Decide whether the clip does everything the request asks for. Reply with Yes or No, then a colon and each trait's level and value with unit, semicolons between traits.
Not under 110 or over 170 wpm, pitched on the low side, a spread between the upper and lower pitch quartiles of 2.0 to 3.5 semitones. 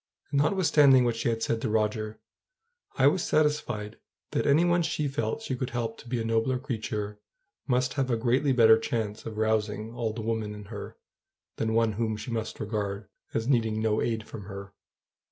No: average, 190 wpm; low, 115 Hz; average, 3.0 semitones